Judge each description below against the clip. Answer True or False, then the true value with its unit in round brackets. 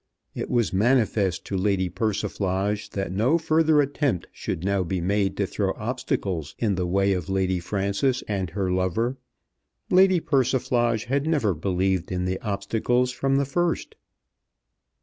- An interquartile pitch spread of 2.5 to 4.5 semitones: False (5.1 semitones)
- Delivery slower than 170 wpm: True (150 wpm)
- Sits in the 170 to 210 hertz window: False (100 Hz)